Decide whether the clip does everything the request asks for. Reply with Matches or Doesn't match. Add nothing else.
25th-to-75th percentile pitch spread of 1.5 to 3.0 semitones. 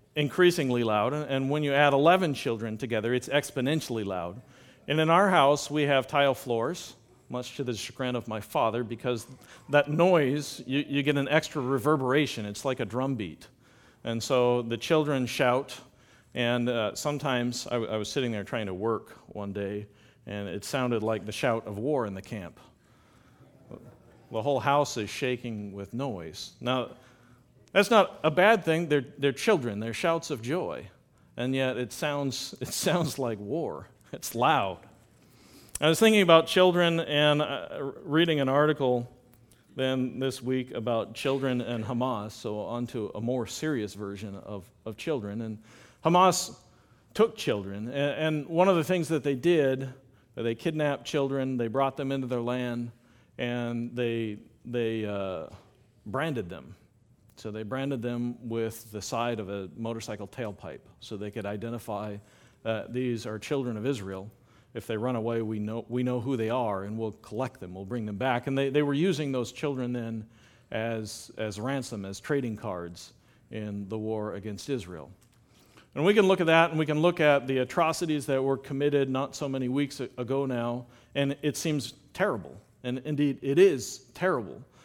Doesn't match